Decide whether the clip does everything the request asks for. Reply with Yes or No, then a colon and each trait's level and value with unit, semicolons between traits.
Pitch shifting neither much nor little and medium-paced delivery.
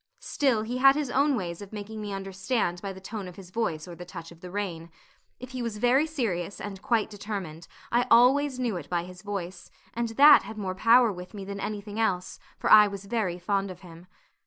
No: average, 4.4 semitones; fast, 225 wpm